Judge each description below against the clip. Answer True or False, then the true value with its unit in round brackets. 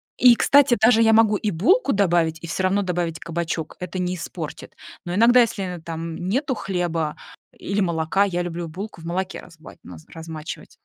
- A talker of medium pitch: True (180 Hz)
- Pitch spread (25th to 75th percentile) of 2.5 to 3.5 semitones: False (3.9 semitones)